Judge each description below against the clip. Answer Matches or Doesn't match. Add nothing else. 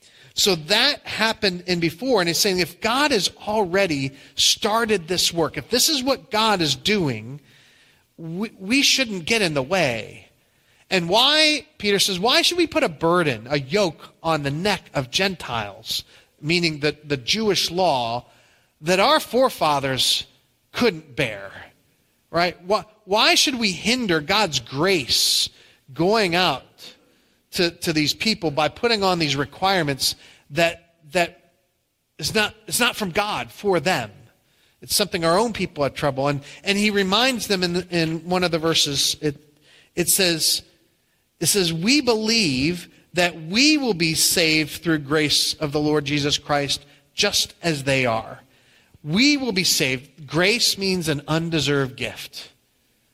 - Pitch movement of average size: Doesn't match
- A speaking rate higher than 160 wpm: Doesn't match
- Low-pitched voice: Doesn't match